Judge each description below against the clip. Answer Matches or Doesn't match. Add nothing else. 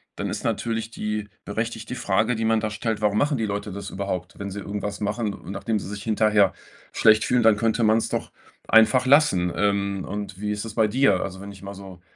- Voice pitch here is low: Matches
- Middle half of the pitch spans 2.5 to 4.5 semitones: Doesn't match